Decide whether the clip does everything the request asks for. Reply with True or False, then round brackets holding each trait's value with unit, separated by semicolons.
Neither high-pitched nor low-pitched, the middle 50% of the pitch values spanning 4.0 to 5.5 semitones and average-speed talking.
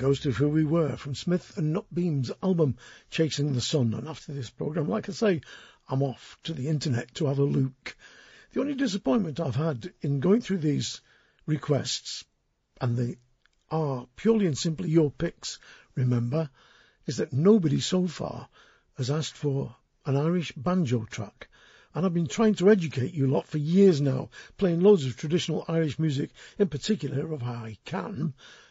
True (155 Hz; 4.6 semitones; 175 wpm)